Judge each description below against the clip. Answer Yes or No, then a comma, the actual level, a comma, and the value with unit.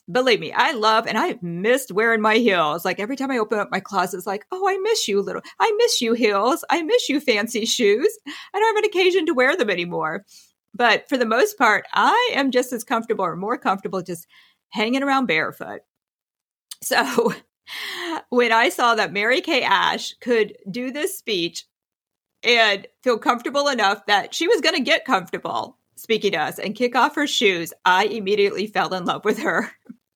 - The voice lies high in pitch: Yes, high, 240 Hz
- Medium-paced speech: Yes, average, 195 wpm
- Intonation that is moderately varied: No, wide, 6.5 semitones